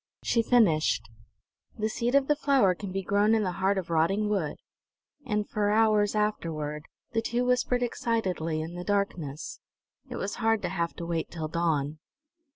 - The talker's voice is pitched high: Yes, high, 200 Hz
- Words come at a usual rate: Yes, average, 170 wpm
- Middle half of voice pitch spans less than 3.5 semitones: No, average, 5.1 semitones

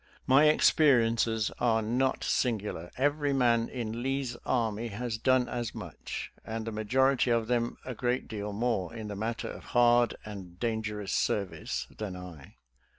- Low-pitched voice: Yes, low, 115 Hz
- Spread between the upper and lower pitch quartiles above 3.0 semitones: No, average, 2.7 semitones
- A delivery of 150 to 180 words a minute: Yes, average, 155 wpm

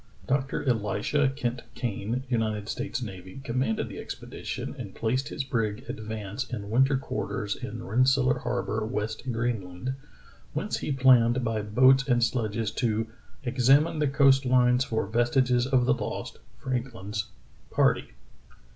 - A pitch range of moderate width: Yes, average, 3.2 semitones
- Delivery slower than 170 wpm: Yes, average, 145 wpm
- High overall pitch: No, low, 120 Hz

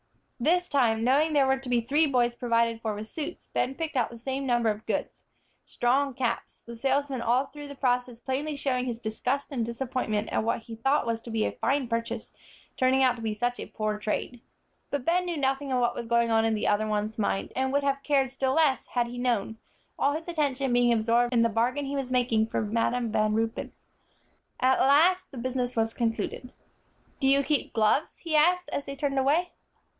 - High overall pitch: Yes, very high, 250 Hz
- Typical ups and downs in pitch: Yes, average, 3.2 semitones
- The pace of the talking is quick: Yes, fast, 215 wpm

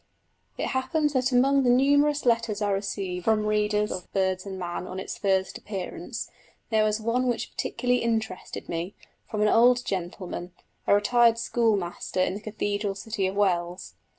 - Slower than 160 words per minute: No, average, 165 wpm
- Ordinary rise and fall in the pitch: Yes, average, 4.1 semitones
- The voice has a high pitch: Yes, high, 210 Hz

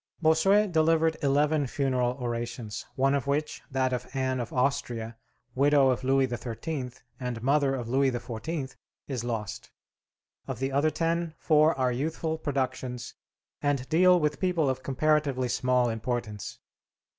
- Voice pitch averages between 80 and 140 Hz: Yes, low, 135 Hz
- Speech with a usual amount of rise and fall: Yes, average, 3.6 semitones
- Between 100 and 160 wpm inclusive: Yes, average, 140 wpm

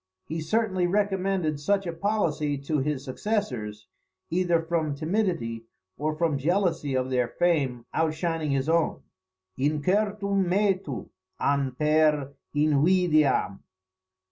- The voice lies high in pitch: No, medium, 155 Hz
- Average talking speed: No, slow, 110 wpm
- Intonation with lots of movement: No, average, 4.7 semitones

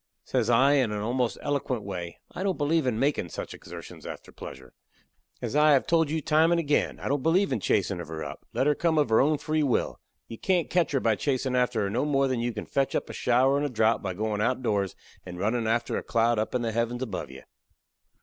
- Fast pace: Yes, fast, 245 wpm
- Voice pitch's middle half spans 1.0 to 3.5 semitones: No, average, 4.9 semitones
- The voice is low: Yes, low, 125 Hz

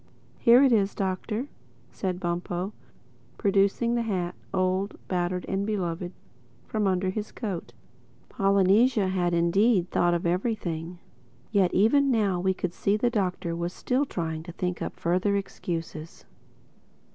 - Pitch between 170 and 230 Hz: Yes, high, 190 Hz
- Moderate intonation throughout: Yes, average, 3.1 semitones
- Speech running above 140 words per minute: No, slow, 135 wpm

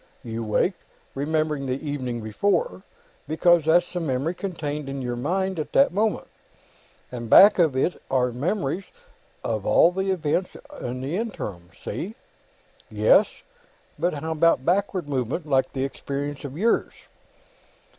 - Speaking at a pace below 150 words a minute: Yes, average, 140 wpm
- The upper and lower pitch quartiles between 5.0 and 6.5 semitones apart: Yes, wide, 5.4 semitones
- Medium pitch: Yes, medium, 150 Hz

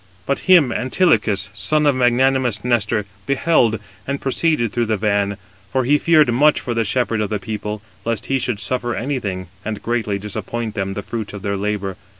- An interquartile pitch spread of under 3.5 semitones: No, average, 4.0 semitones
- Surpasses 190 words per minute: No, average, 185 wpm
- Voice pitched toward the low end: Yes, low, 115 Hz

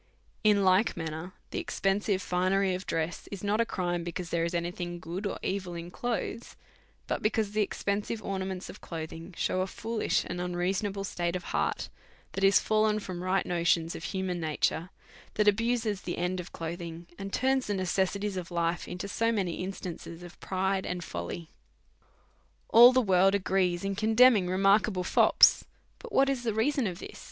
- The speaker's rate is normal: Yes, average, 180 wpm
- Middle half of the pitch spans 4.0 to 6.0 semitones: No, average, 2.9 semitones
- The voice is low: No, high, 190 Hz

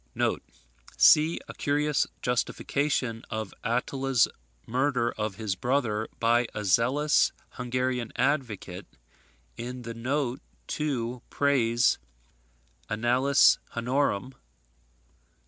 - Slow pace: Yes, slow, 90 wpm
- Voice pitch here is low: Yes, low, 125 Hz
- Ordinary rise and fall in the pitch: Yes, average, 3.1 semitones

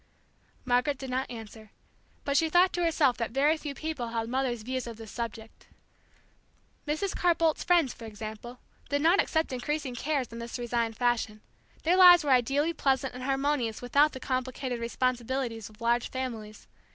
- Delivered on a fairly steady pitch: No, average, 4.0 semitones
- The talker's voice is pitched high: Yes, very high, 255 Hz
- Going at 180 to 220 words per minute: No, average, 170 wpm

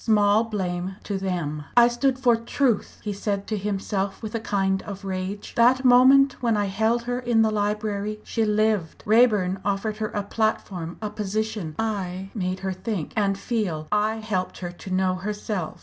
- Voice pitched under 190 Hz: No, high, 210 Hz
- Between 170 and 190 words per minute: Yes, average, 180 wpm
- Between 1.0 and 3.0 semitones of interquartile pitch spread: Yes, average, 2.7 semitones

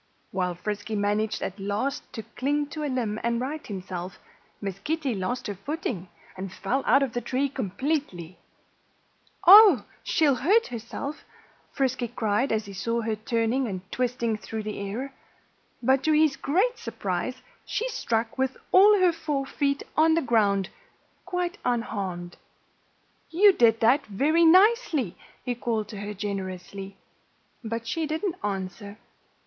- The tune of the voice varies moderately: No, wide, 6.3 semitones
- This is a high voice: Yes, high, 235 Hz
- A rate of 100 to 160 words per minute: Yes, average, 145 wpm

